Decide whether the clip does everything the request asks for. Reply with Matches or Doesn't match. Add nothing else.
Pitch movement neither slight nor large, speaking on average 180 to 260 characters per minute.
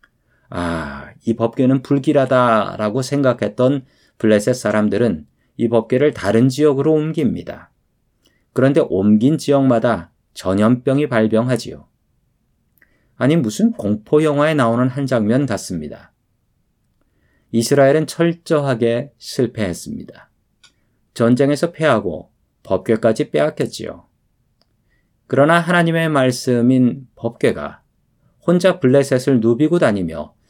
Matches